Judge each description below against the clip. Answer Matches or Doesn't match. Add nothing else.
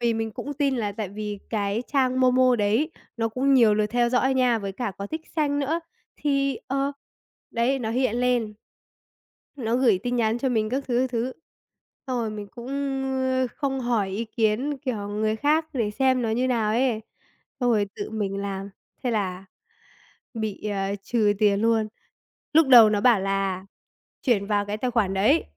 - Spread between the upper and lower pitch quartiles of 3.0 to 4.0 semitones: Matches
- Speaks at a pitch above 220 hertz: Matches